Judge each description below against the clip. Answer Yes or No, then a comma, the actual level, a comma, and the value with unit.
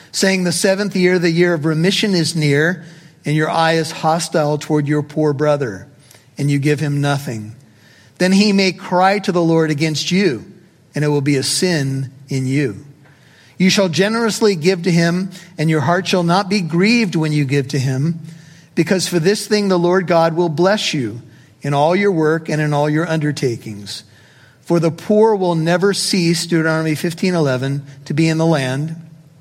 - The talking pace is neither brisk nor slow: Yes, average, 190 wpm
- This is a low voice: No, medium, 160 Hz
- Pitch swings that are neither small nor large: Yes, average, 3.9 semitones